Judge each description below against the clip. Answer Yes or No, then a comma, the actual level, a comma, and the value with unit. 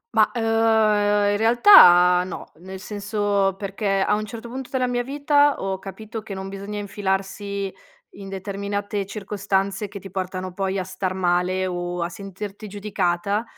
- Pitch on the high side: Yes, high, 200 Hz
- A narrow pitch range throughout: Yes, narrow, 1.8 semitones